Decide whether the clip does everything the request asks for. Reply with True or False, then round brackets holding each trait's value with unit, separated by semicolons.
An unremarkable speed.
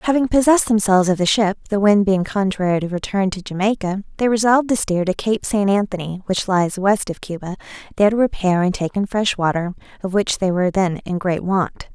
False (215 wpm)